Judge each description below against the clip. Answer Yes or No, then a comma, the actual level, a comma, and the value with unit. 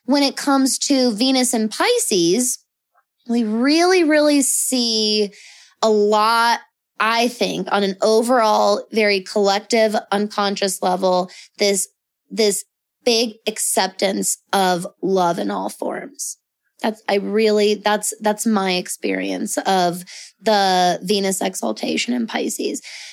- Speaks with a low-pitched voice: No, high, 215 Hz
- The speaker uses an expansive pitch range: No, average, 3.3 semitones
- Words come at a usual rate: No, slow, 115 wpm